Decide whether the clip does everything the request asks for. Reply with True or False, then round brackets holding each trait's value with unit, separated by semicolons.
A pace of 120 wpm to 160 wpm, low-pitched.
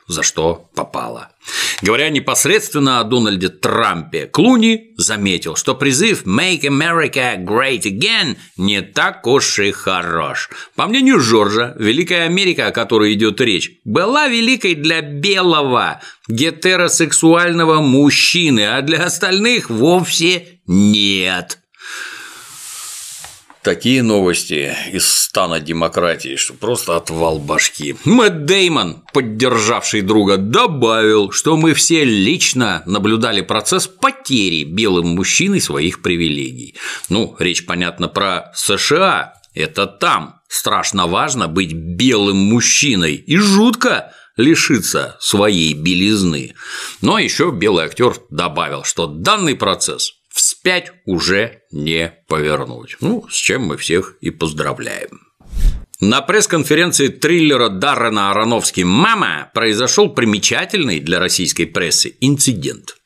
False (110 wpm; 125 Hz)